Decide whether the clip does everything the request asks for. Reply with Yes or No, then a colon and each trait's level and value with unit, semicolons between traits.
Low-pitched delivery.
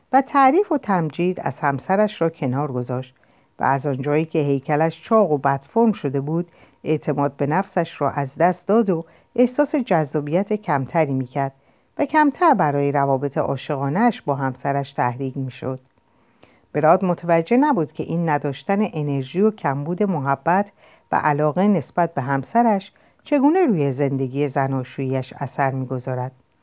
No: medium, 150 Hz